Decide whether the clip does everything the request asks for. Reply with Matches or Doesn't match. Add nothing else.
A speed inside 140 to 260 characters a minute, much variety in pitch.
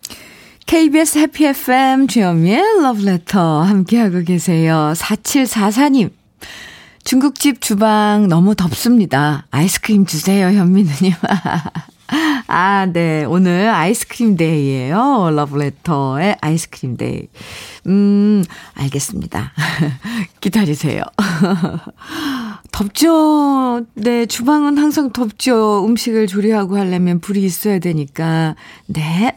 Matches